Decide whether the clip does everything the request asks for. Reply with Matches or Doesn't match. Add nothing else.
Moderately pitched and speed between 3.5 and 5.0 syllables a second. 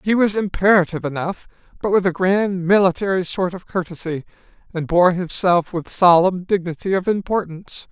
Doesn't match